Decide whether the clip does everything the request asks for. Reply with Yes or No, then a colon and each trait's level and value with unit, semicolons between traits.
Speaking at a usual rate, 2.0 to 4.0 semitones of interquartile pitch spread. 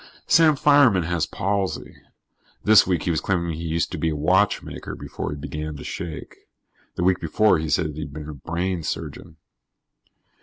Yes: average, 175 wpm; average, 3.5 semitones